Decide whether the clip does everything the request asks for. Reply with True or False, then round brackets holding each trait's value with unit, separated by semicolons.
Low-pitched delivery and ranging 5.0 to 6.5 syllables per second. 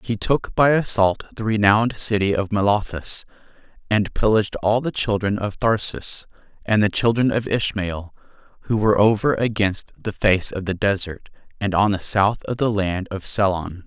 True (105 Hz; 5.1 syllables/s)